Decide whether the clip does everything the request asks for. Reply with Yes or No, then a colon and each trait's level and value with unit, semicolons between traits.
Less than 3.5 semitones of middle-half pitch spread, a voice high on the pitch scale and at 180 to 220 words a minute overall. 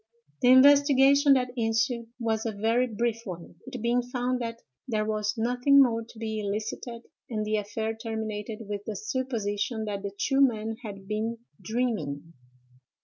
No: narrow, 2.6 semitones; high, 225 Hz; average, 155 wpm